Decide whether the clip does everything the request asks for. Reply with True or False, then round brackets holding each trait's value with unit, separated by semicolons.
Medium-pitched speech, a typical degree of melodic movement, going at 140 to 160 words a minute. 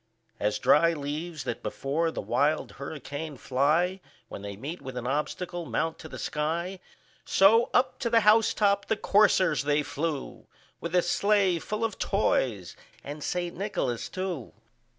True (165 Hz; 5.0 semitones; 155 wpm)